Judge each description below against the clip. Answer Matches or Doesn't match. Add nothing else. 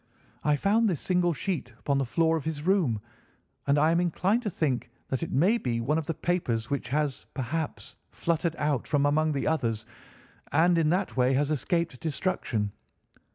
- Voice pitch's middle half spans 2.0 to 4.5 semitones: Matches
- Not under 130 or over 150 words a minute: Doesn't match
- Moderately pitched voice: Matches